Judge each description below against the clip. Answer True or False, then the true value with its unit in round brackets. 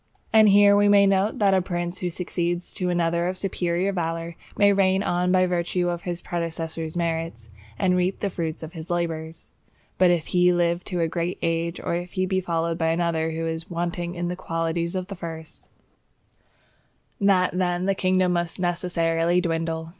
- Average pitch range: False (1.8 semitones)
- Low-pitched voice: False (175 Hz)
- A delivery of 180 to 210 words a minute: True (185 wpm)